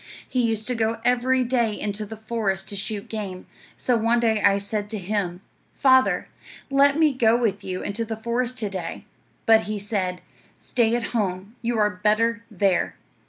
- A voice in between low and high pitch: No, high, 220 Hz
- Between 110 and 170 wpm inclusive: No, average, 180 wpm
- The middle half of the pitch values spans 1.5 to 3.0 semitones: Yes, average, 2.7 semitones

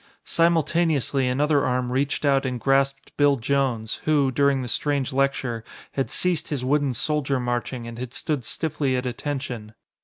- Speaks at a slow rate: No, average, 155 wpm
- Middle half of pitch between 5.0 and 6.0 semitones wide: No, narrow, 2.4 semitones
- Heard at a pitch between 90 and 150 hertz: Yes, low, 135 Hz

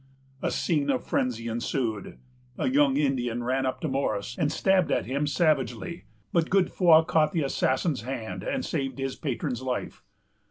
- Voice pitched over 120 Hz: Yes, low, 135 Hz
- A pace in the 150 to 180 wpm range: Yes, average, 160 wpm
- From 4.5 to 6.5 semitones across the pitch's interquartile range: No, average, 4.0 semitones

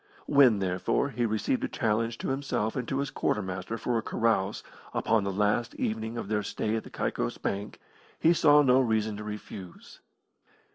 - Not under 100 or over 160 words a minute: No, average, 180 wpm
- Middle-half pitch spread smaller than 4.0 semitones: Yes, average, 3.0 semitones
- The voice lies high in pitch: No, low, 110 Hz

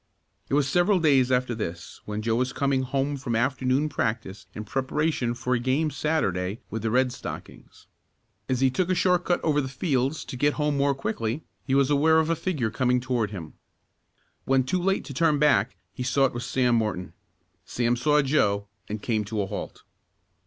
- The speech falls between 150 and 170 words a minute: No, average, 195 wpm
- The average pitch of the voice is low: Yes, low, 130 Hz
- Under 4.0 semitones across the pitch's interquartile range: No, average, 4.3 semitones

